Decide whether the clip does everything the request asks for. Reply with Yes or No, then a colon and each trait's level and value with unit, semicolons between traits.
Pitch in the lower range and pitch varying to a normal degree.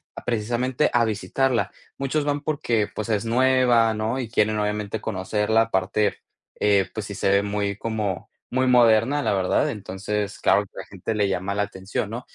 Yes: low, 110 Hz; average, 3.0 semitones